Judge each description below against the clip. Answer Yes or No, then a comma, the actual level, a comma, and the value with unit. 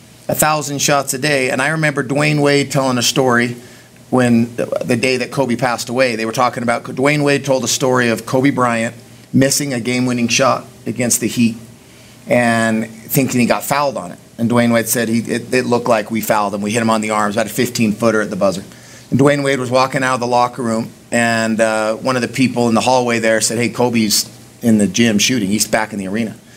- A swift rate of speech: Yes, fast, 235 wpm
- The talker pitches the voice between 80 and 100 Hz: No, low, 120 Hz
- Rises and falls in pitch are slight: Yes, narrow, 2.3 semitones